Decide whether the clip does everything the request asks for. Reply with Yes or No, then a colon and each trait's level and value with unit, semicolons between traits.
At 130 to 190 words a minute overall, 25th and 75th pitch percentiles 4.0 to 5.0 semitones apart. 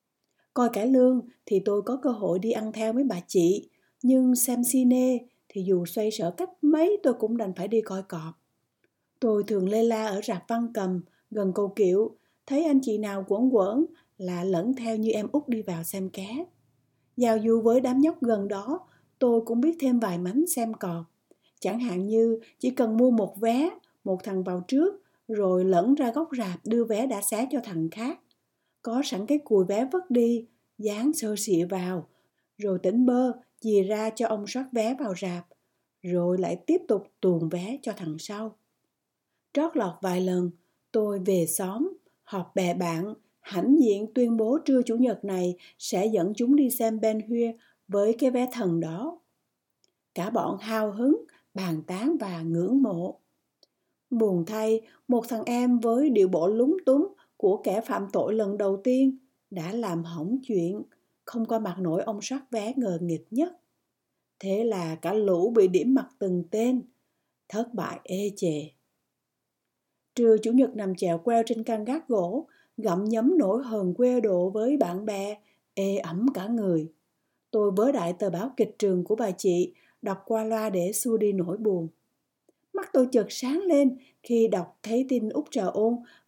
Yes: average, 185 wpm; average, 4.7 semitones